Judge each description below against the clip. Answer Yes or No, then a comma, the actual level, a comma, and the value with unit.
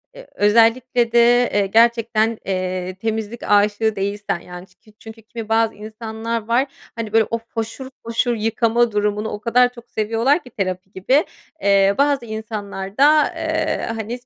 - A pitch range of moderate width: No, narrow, 2.3 semitones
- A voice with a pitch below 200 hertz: No, high, 225 Hz